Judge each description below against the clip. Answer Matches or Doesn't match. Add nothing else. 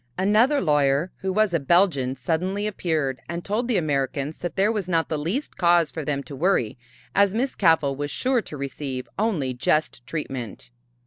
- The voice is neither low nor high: Matches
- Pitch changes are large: Matches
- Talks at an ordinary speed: Matches